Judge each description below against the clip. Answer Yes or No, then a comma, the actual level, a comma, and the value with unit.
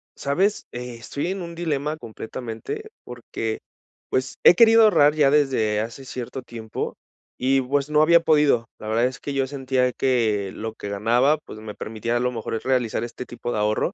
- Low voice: Yes, low, 130 Hz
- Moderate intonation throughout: Yes, average, 4.5 semitones